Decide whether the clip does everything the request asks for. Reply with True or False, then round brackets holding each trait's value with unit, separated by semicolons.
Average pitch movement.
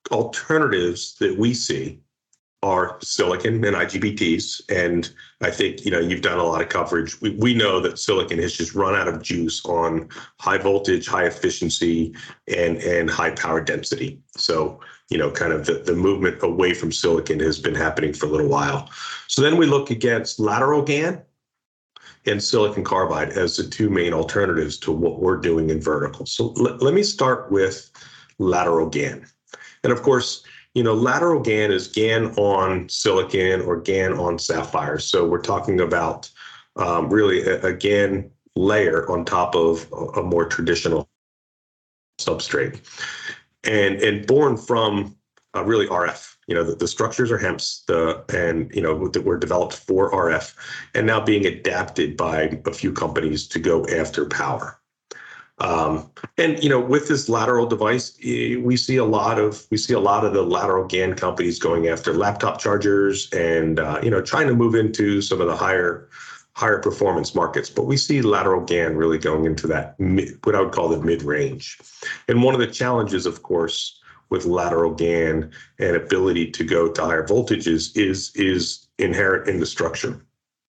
False (6.2 semitones)